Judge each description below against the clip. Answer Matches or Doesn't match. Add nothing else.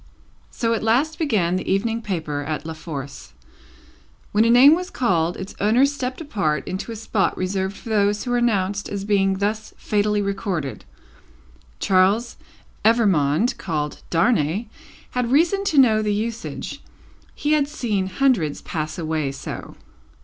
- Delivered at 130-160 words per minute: Matches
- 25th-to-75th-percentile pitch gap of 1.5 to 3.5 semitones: Doesn't match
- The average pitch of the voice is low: Doesn't match